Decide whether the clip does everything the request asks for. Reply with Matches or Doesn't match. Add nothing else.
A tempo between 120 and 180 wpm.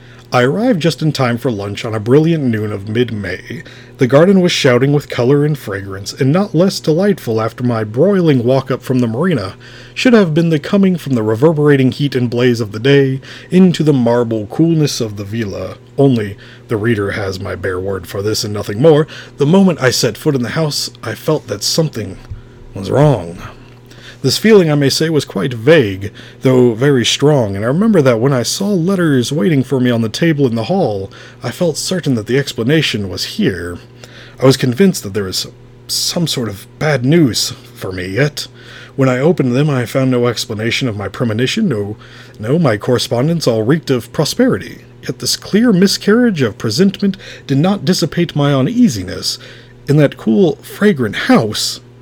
Doesn't match